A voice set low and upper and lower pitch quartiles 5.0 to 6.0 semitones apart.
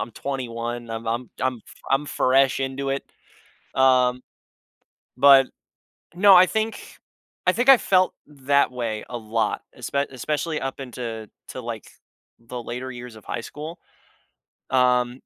No: low, 130 Hz; average, 2.9 semitones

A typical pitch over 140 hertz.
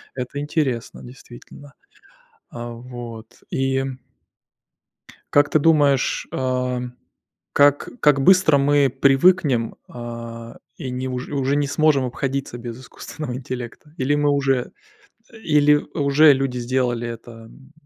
No: low, 135 Hz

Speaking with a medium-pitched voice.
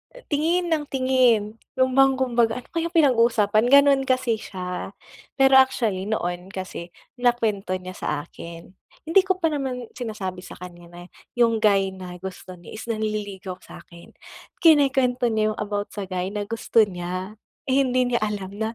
No: high, 220 Hz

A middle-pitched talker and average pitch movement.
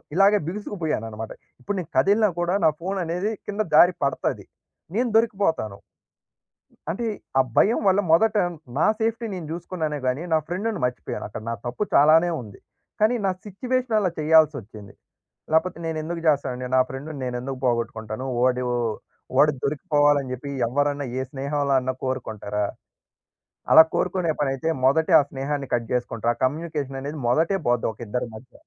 No: medium, 150 Hz; wide, 6.1 semitones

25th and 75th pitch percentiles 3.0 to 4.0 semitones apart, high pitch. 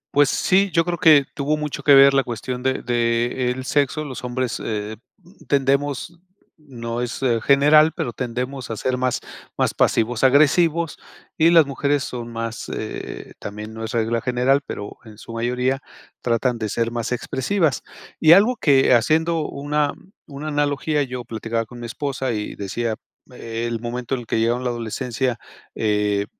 No: average, 3.7 semitones; low, 125 Hz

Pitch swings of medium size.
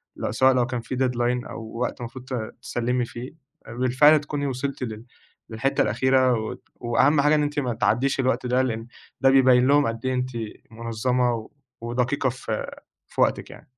No: narrow, 1.9 semitones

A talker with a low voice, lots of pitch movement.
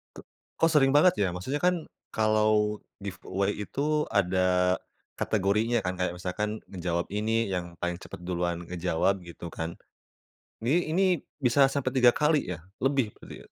Yes: low, 105 Hz; wide, 5.9 semitones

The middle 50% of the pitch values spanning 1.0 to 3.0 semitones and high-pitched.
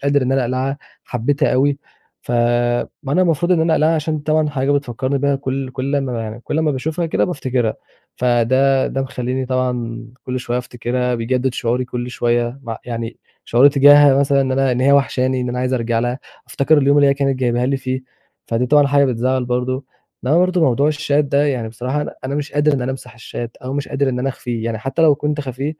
No: narrow, 2.4 semitones; low, 130 Hz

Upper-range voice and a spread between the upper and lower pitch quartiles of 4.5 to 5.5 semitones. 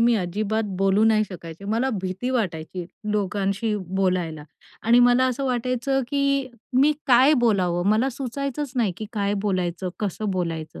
Yes: high, 215 Hz; average, 5.1 semitones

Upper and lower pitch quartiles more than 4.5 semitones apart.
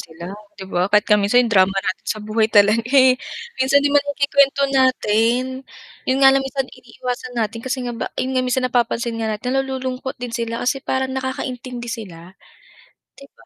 No: average, 3.2 semitones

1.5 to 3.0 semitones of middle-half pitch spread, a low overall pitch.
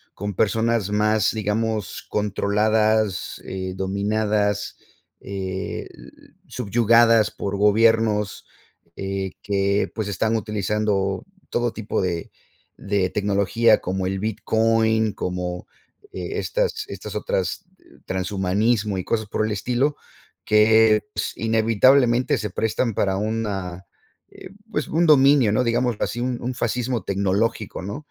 Yes: narrow, 2.4 semitones; low, 105 Hz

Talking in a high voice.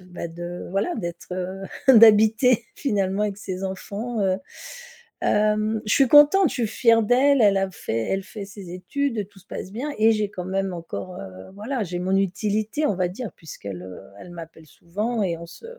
Yes: high, 200 Hz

